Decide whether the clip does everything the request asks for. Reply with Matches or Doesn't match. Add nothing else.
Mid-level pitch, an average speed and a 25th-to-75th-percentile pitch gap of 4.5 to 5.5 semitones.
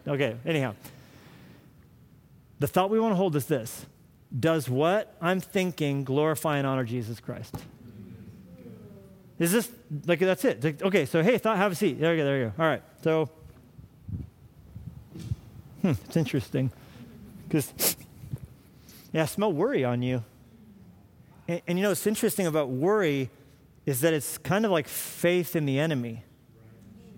Matches